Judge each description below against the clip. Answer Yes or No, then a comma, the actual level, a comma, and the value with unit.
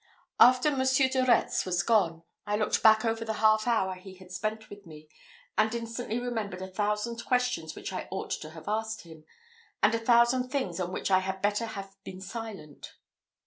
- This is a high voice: Yes, high, 215 Hz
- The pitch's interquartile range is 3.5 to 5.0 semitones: Yes, average, 3.8 semitones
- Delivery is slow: No, average, 190 wpm